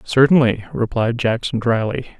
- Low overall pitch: Yes, low, 120 Hz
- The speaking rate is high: No, slow, 110 wpm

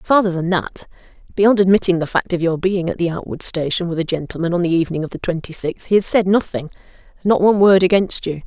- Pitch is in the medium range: Yes, medium, 180 Hz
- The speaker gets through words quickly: Yes, fast, 215 wpm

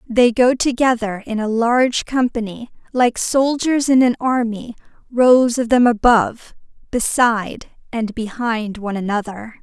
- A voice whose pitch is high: Yes, high, 235 Hz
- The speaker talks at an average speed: No, slow, 130 wpm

